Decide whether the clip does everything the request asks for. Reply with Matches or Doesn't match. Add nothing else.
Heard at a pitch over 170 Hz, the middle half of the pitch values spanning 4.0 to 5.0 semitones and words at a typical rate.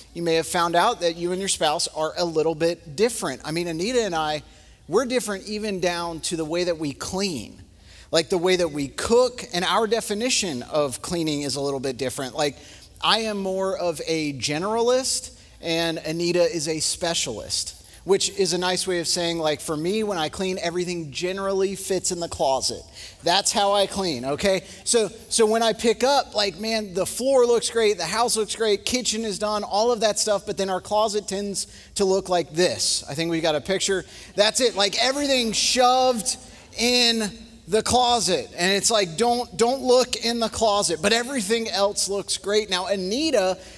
Matches